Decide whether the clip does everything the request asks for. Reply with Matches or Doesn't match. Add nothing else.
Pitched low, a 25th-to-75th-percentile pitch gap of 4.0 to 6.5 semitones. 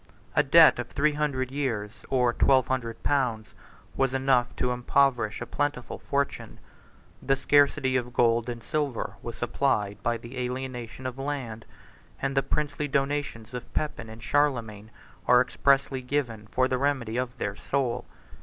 Doesn't match